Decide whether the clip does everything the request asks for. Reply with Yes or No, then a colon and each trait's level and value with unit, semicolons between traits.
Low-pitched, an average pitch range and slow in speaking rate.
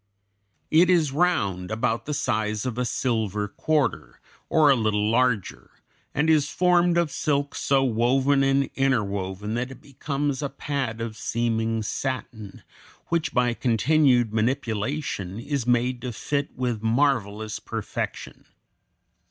Yes: low, 125 Hz; average, 4.4 semitones; slow, 130 wpm